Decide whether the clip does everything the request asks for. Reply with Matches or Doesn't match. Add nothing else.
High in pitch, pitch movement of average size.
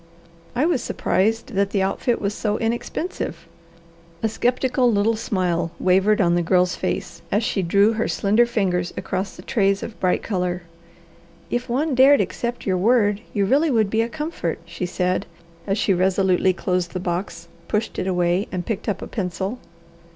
Matches